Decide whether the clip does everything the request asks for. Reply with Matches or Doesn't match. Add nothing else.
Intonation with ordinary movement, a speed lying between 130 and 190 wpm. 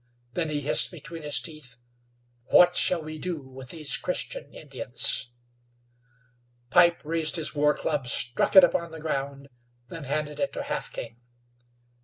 Matches